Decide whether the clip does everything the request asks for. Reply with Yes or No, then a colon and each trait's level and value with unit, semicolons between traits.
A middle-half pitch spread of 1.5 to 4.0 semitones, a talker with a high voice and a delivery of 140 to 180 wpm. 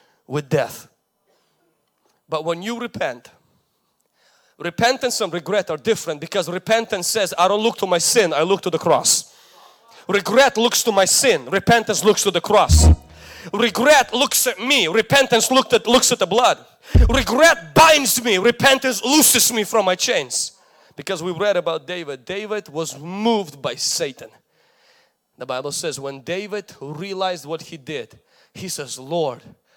No: wide, 5.5 semitones; high, 200 Hz; average, 155 wpm